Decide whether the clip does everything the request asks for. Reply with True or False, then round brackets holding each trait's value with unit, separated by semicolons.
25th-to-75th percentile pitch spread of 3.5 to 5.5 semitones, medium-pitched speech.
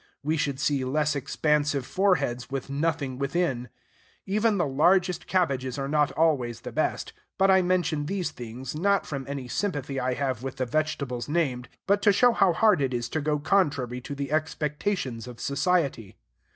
True (5.1 semitones; 145 Hz)